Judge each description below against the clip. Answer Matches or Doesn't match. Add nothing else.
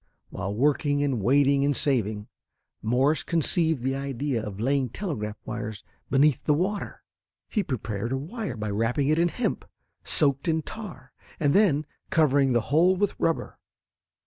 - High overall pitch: Doesn't match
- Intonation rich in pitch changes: Doesn't match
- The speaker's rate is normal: Matches